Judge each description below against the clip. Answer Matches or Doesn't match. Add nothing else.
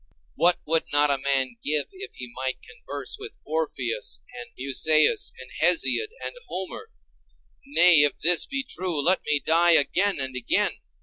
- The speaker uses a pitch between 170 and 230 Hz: Doesn't match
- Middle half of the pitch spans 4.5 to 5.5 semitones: Matches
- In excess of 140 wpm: Matches